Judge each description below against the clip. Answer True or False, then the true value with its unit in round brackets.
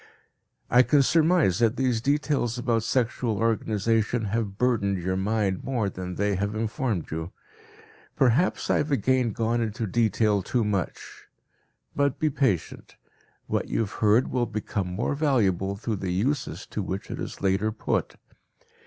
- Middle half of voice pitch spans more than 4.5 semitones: False (4.1 semitones)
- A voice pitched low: True (110 Hz)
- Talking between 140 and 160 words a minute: True (155 wpm)